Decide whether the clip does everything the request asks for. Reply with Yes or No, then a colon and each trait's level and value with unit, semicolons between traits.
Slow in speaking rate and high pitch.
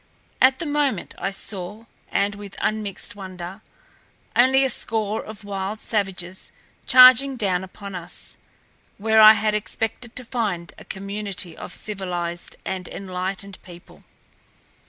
Yes: slow, 130 wpm; high, 200 Hz